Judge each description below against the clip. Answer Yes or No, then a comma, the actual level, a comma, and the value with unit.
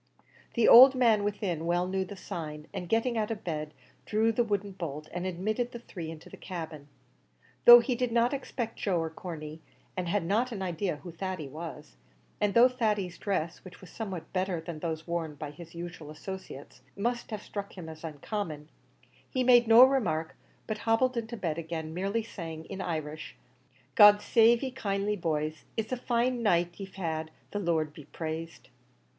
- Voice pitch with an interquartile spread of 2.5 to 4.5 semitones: No, wide, 5.6 semitones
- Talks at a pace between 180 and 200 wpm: Yes, average, 185 wpm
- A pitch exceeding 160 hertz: Yes, medium, 185 Hz